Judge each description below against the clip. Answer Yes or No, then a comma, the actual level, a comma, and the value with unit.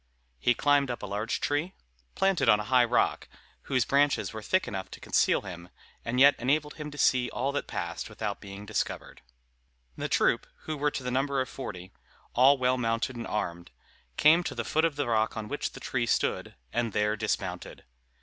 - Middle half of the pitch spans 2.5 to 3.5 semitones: No, average, 4.8 semitones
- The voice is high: No, low, 125 Hz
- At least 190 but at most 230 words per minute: Yes, average, 200 wpm